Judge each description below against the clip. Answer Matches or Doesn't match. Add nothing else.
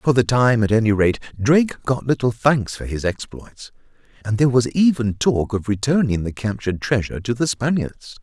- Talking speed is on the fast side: Doesn't match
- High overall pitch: Doesn't match